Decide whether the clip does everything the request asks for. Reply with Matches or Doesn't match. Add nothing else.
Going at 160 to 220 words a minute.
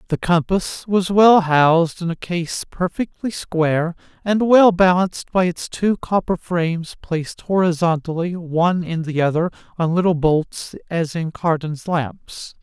Doesn't match